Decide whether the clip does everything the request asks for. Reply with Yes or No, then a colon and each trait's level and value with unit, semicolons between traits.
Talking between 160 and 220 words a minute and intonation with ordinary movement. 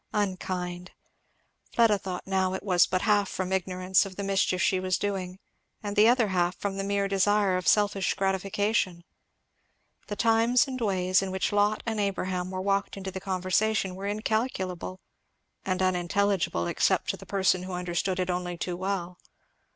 No: average, 165 wpm; narrow, 1.8 semitones